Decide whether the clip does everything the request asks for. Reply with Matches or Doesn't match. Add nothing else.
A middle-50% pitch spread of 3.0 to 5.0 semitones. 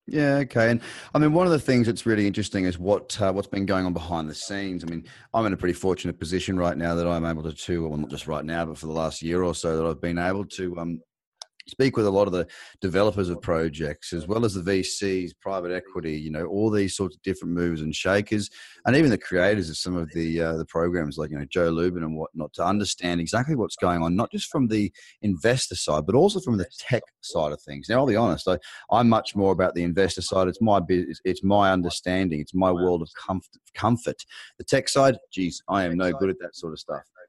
Matches